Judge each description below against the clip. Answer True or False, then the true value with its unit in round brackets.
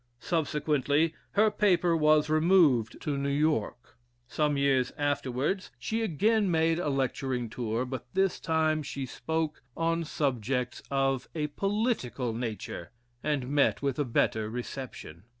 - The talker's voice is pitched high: False (145 Hz)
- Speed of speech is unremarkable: False (130 wpm)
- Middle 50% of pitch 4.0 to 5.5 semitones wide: True (4.3 semitones)